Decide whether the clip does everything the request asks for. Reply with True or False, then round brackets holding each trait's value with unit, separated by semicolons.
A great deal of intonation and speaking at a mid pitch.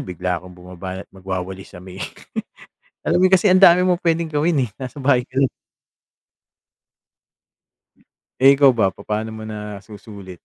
False (7.4 semitones; 110 Hz)